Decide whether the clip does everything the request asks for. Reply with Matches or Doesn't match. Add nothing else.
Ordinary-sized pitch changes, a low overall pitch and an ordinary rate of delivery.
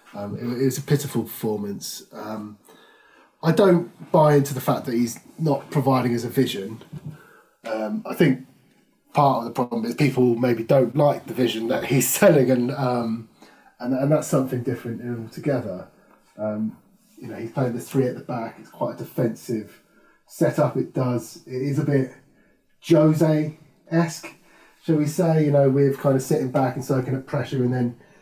Matches